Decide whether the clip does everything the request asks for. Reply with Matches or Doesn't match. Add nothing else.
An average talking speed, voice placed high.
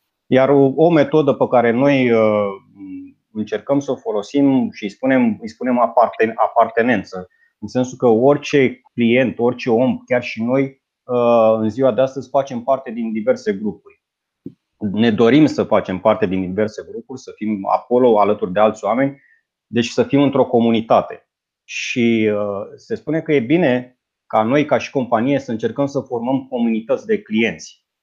Doesn't match